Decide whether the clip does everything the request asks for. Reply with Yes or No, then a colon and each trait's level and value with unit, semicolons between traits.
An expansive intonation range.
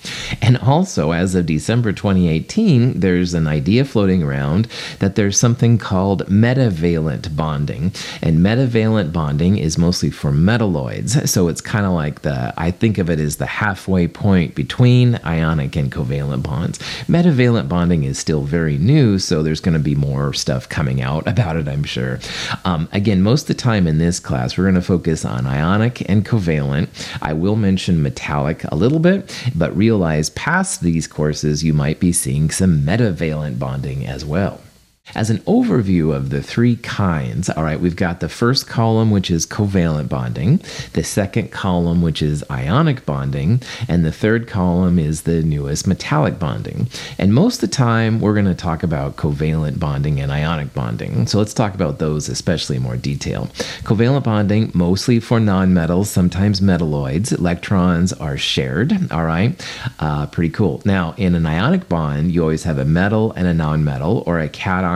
Yes: wide, 6.1 semitones